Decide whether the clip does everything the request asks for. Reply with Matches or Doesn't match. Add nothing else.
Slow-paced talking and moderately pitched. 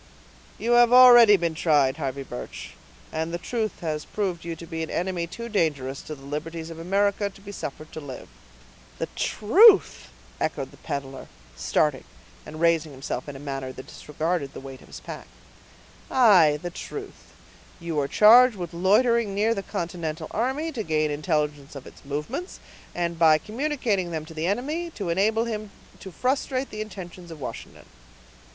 Doesn't match